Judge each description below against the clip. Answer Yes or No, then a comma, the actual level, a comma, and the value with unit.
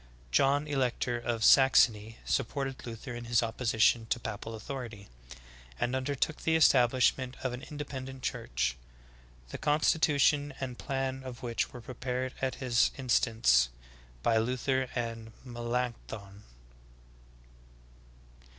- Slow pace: Yes, slow, 115 wpm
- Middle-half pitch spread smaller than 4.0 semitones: Yes, average, 2.7 semitones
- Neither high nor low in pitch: No, low, 125 Hz